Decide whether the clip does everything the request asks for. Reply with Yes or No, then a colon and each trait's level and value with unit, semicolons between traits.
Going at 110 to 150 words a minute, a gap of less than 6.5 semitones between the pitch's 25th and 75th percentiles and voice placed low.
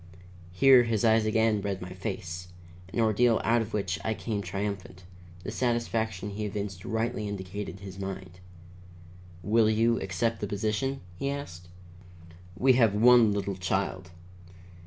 Yes: average, 140 wpm; average, 3.1 semitones; low, 105 Hz